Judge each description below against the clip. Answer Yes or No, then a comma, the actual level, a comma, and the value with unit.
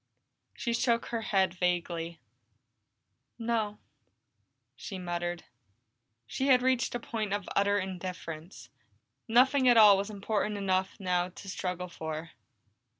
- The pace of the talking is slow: Yes, slow, 120 wpm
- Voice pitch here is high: Yes, high, 195 Hz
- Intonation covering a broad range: No, average, 4.1 semitones